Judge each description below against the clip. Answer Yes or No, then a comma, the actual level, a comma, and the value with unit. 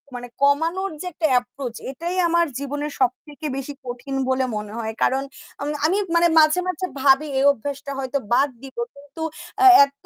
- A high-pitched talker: Yes, very high, 280 Hz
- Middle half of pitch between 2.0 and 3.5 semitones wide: Yes, average, 3.2 semitones